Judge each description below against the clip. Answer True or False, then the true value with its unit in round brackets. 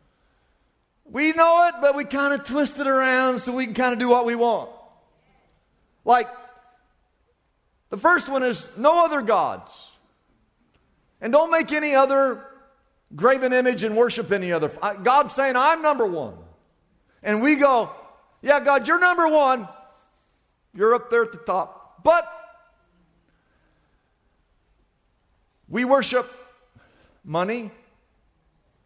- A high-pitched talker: True (265 Hz)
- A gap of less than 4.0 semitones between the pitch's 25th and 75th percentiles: True (3.2 semitones)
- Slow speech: True (125 wpm)